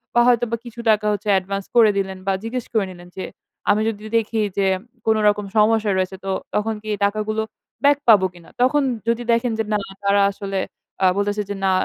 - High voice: Yes, high, 210 Hz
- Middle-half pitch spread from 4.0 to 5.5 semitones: No, narrow, 2.4 semitones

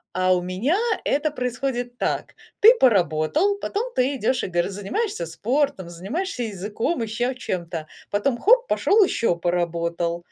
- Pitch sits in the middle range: No, high, 225 Hz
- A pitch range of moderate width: No, wide, 7.9 semitones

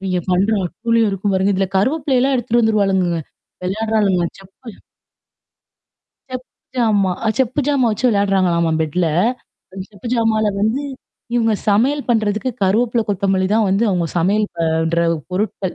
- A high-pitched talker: Yes, high, 205 Hz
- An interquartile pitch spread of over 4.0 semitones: No, average, 3.4 semitones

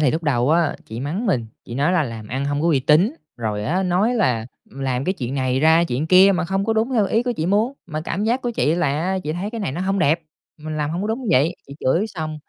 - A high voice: No, medium, 165 Hz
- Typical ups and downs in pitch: No, wide, 5.9 semitones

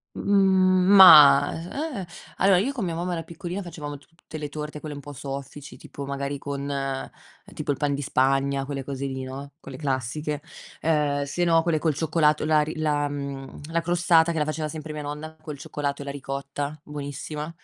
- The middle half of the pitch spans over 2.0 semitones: Yes, narrow, 2.6 semitones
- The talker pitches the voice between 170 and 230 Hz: No, medium, 150 Hz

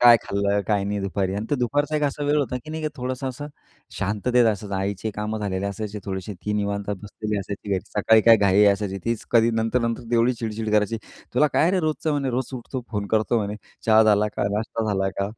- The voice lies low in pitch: Yes, low, 110 Hz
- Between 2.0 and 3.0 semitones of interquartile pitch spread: No, average, 3.4 semitones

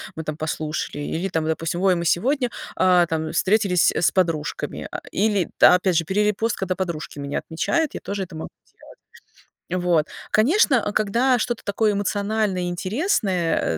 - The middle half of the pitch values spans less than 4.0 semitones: No, average, 4.5 semitones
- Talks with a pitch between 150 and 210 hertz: Yes, medium, 185 Hz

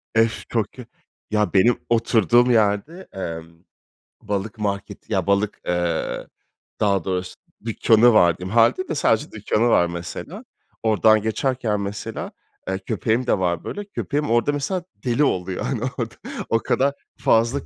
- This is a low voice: Yes, low, 110 Hz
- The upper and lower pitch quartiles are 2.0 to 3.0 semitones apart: No, average, 3.7 semitones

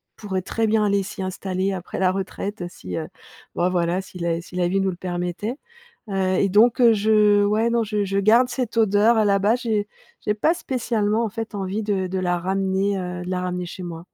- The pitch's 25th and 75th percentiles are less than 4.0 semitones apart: Yes, average, 2.9 semitones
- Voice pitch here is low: No, high, 200 Hz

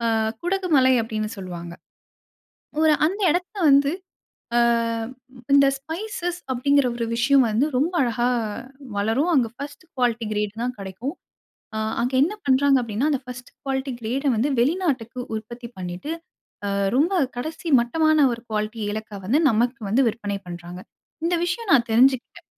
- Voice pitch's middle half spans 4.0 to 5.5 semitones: Yes, average, 4.4 semitones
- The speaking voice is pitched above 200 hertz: Yes, very high, 250 Hz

